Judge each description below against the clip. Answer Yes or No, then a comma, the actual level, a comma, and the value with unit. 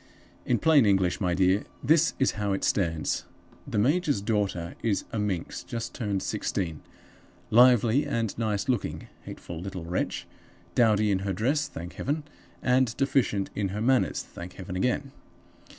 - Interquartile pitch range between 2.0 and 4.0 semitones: No, average, 5.0 semitones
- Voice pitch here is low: Yes, low, 105 Hz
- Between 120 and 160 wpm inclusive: Yes, average, 150 wpm